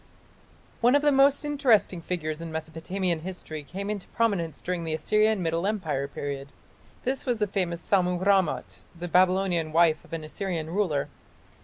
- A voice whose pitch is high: No, medium, 180 Hz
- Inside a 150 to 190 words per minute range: Yes, average, 160 wpm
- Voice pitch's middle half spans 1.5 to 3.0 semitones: No, average, 4.1 semitones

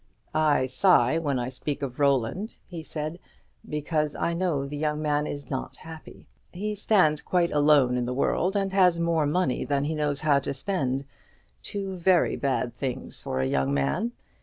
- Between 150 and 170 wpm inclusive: No, average, 180 wpm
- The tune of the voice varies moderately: Yes, average, 4.0 semitones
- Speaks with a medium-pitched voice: Yes, medium, 150 Hz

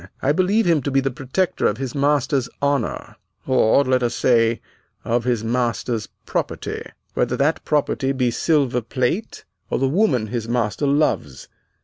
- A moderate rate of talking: Yes, average, 155 wpm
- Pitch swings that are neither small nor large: Yes, average, 3.3 semitones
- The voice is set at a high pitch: No, low, 130 Hz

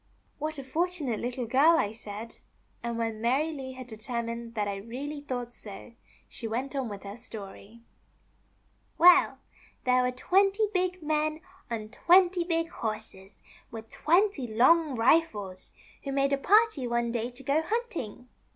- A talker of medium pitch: No, very high, 255 Hz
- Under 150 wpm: No, average, 165 wpm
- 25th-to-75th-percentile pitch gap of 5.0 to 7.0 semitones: Yes, wide, 5.6 semitones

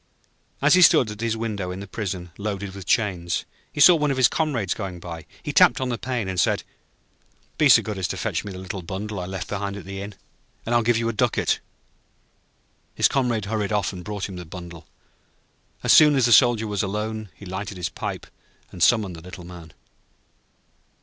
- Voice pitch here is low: Yes, low, 100 Hz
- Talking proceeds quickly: Yes, fast, 215 wpm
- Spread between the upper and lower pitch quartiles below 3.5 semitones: No, average, 3.8 semitones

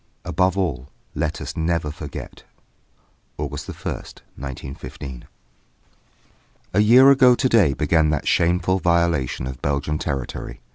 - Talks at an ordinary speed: No, slow, 125 wpm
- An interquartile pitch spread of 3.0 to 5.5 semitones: Yes, average, 4.9 semitones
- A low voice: Yes, very low, 80 Hz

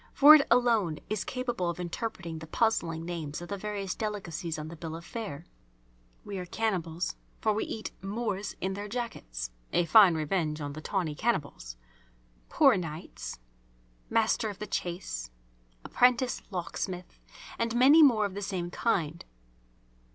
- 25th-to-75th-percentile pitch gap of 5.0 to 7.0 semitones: Yes, average, 5.3 semitones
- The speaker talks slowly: No, average, 150 wpm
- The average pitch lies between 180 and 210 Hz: Yes, high, 190 Hz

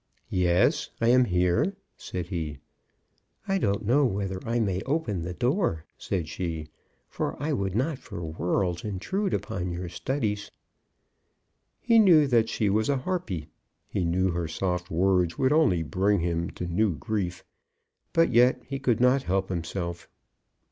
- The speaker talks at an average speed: Yes, average, 155 wpm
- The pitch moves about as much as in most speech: No, wide, 6.4 semitones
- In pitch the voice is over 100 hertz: No, very low, 95 Hz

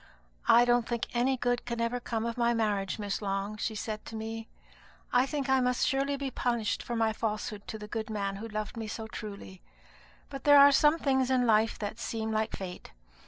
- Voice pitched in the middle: No, high, 225 Hz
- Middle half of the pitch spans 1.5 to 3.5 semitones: Yes, narrow, 2.5 semitones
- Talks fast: Yes, fast, 210 wpm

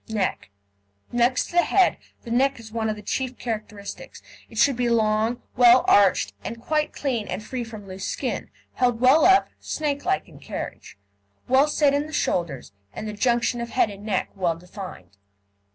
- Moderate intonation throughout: Yes, average, 3.9 semitones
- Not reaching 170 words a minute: No, average, 180 wpm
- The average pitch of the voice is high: Yes, high, 235 Hz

